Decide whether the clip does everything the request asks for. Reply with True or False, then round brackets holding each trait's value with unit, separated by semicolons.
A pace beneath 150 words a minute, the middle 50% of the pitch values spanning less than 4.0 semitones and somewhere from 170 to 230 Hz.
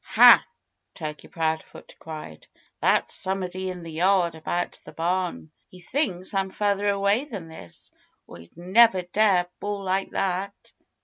True (140 wpm; 3.0 semitones; 185 Hz)